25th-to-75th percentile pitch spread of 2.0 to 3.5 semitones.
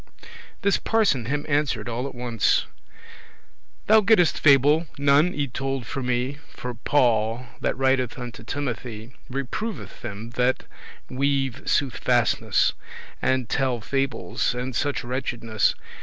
Yes: average, 2.8 semitones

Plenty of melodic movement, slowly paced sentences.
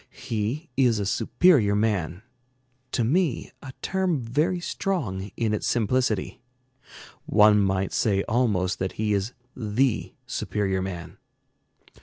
No: average, 4.8 semitones; slow, 120 wpm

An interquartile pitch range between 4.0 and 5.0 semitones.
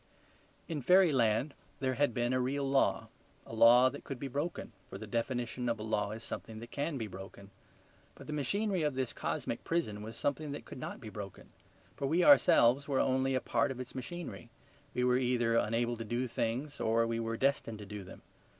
No: average, 3.6 semitones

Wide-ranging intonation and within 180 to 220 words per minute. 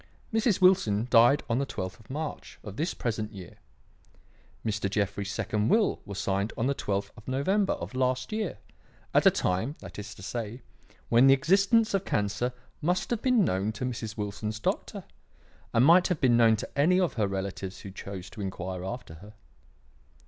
Yes: wide, 6.0 semitones; average, 185 wpm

